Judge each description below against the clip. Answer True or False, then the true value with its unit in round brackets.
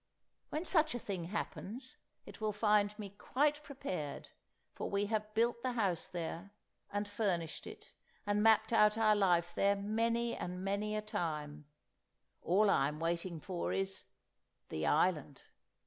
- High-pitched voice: True (205 Hz)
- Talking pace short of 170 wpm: True (145 wpm)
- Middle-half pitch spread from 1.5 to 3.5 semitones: False (3.9 semitones)